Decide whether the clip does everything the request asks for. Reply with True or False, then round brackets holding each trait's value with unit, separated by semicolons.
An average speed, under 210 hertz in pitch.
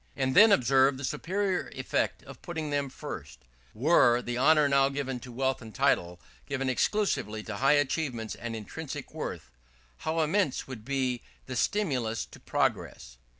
True (155 wpm; 135 Hz)